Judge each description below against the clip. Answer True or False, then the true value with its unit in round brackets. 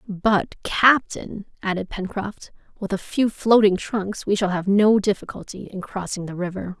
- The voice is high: True (200 Hz)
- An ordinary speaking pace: True (160 wpm)